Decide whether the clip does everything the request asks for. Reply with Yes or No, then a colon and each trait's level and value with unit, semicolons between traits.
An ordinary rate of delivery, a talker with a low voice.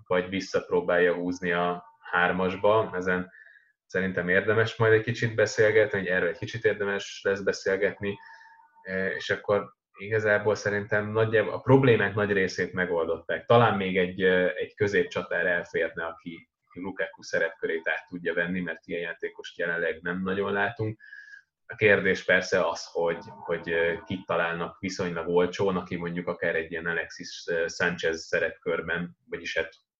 Yes: average, 140 wpm; low, 110 Hz